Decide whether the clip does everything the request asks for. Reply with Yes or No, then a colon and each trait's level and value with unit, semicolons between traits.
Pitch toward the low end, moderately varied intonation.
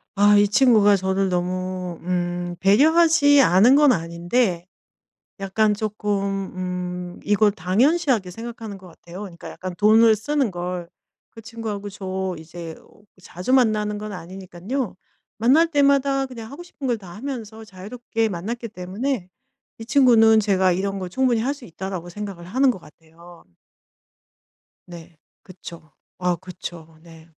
No: high, 200 Hz; average, 4.5 semitones